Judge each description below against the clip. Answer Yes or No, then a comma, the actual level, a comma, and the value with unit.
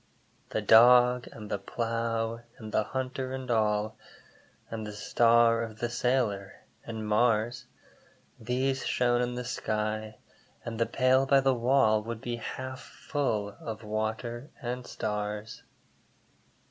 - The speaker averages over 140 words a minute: No, slow, 135 wpm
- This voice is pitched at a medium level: No, low, 115 Hz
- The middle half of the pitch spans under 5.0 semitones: Yes, narrow, 2.4 semitones